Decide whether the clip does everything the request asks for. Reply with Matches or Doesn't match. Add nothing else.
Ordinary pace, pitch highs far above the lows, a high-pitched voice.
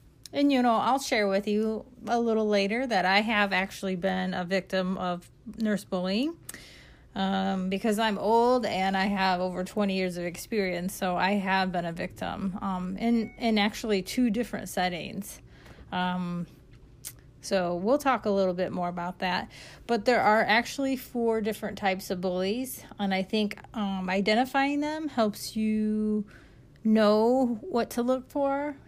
Doesn't match